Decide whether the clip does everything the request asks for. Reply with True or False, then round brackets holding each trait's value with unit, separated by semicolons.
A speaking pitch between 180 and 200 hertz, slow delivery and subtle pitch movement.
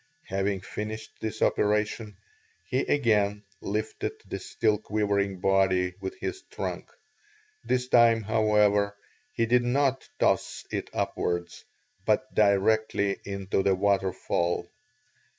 False (105 Hz; 110 wpm; 2.1 semitones)